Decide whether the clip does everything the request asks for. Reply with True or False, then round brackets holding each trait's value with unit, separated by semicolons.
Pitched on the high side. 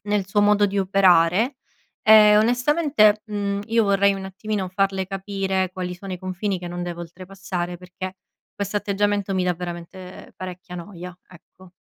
True (195 Hz)